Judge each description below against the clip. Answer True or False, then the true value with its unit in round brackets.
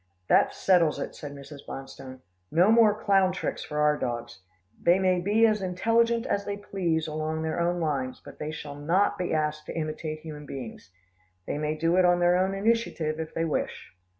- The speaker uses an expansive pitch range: False (4.0 semitones)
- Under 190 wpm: False (195 wpm)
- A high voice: False (165 Hz)